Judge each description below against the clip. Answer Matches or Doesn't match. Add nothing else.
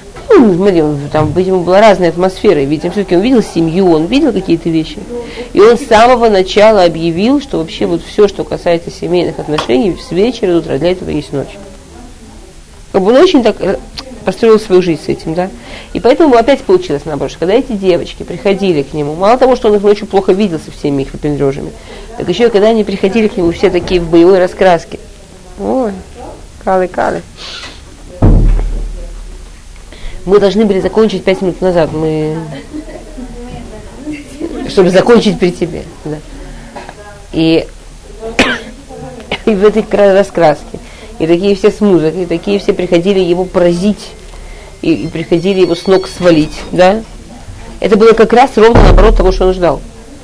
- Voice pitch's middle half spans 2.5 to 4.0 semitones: Doesn't match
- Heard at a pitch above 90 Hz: Matches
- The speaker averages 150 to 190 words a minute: Matches